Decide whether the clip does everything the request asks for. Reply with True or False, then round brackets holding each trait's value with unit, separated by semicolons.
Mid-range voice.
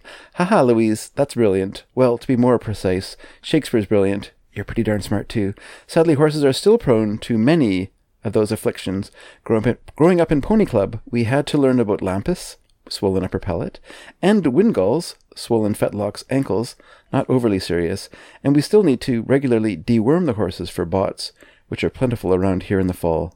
False (115 Hz)